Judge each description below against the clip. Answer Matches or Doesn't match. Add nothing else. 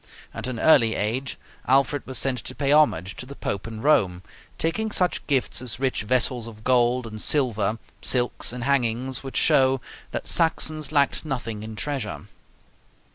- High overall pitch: Doesn't match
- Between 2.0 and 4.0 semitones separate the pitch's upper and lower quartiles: Matches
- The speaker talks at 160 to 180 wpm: Matches